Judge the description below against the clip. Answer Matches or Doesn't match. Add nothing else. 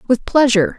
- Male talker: Doesn't match